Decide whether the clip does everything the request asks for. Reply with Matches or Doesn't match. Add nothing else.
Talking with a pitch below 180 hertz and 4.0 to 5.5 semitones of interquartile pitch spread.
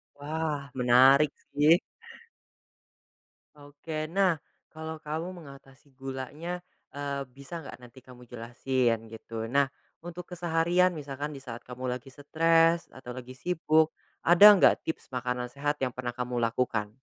Matches